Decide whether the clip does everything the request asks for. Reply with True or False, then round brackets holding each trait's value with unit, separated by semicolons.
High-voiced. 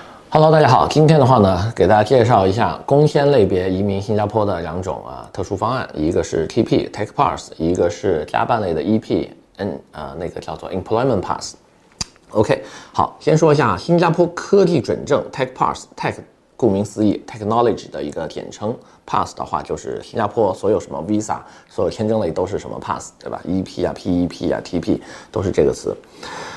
False (130 Hz)